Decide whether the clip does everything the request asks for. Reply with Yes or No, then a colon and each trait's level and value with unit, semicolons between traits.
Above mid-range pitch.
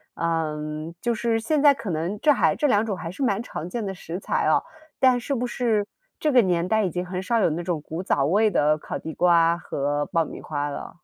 No: medium, 180 Hz